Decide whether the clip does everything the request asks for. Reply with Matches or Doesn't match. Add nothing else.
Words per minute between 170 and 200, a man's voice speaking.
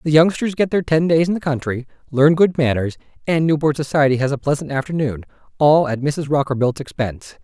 Matches